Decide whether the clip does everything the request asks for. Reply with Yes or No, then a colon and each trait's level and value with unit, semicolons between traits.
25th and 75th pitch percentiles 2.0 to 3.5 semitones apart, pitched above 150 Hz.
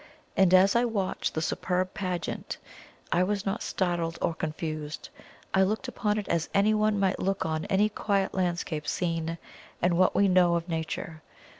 Yes: average, 3.0 semitones; medium, 185 Hz